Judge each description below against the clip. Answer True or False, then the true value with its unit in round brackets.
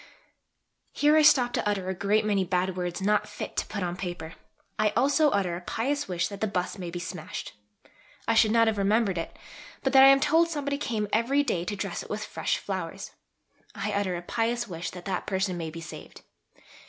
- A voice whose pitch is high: True (205 Hz)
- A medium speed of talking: False (215 wpm)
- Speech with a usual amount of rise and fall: True (5.0 semitones)